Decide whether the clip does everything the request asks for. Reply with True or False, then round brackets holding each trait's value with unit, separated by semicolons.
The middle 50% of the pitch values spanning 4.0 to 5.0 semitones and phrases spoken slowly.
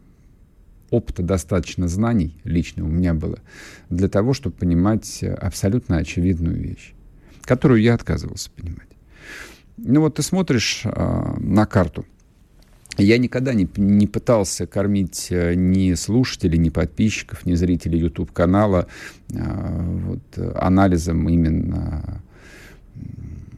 False (3.6 semitones; 105 wpm)